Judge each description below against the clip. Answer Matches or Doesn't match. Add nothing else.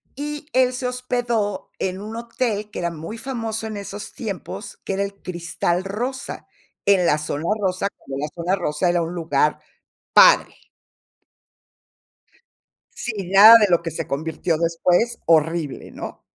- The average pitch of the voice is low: Doesn't match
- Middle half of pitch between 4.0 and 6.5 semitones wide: Matches